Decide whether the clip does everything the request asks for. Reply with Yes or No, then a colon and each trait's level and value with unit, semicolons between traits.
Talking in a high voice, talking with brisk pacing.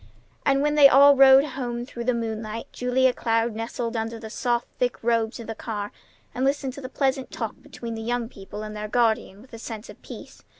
Yes: high, 235 Hz; fast, 215 wpm